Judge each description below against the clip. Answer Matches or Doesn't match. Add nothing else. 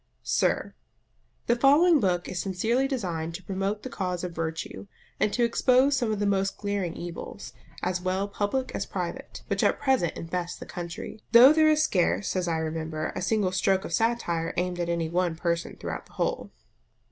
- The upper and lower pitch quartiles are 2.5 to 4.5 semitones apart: Doesn't match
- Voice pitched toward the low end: Doesn't match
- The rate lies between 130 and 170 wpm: Doesn't match